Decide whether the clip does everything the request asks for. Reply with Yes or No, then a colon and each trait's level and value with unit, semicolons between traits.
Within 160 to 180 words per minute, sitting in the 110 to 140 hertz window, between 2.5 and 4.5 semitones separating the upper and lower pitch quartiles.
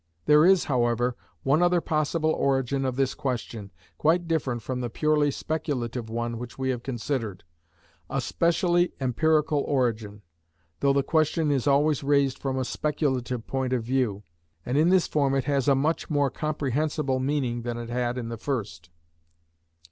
Yes: average, 165 wpm; low, 135 Hz; average, 3.7 semitones